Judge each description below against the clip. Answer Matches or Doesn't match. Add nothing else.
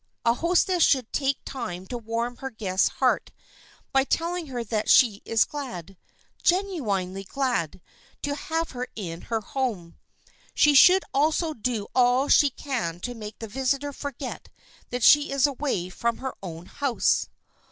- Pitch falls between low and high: Doesn't match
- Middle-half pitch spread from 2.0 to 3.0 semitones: Doesn't match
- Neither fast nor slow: Matches